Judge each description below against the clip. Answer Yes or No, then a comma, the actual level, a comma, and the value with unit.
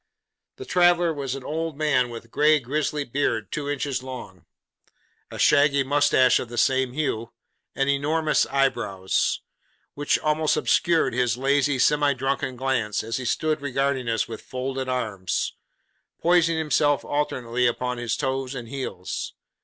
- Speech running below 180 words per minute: Yes, average, 145 wpm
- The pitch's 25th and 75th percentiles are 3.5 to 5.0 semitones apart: No, average, 3.0 semitones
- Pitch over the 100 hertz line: Yes, low, 135 Hz